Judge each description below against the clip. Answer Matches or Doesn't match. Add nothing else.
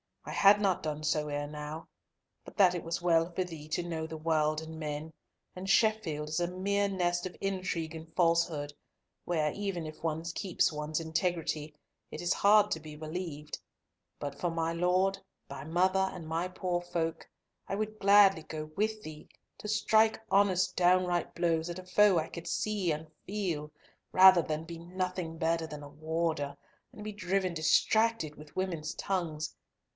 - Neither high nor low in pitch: Matches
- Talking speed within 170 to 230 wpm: Matches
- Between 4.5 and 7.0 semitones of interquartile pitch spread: Doesn't match